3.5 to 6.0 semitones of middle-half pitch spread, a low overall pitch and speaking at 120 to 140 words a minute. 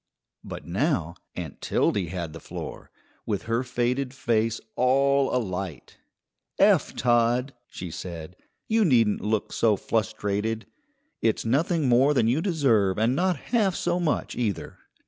Yes: average, 5.1 semitones; low, 120 Hz; slow, 135 wpm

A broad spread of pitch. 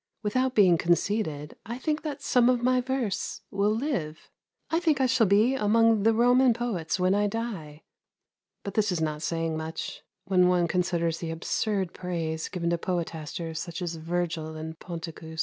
Yes: wide, 5.7 semitones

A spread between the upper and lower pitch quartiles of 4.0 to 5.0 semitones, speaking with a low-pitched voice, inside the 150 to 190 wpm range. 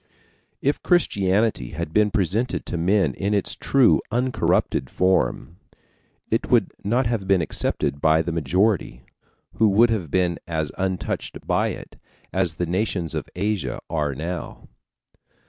No: average, 4.6 semitones; very low, 95 Hz; average, 140 wpm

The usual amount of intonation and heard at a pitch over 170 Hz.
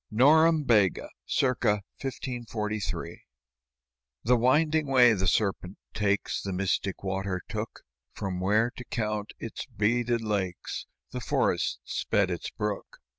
No: average, 3.9 semitones; low, 105 Hz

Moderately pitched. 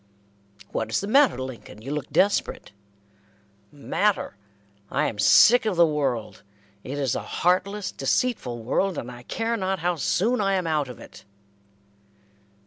Yes: medium, 165 Hz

